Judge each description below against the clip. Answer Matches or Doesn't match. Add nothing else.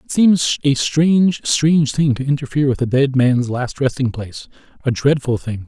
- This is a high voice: Doesn't match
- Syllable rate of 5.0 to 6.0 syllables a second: Matches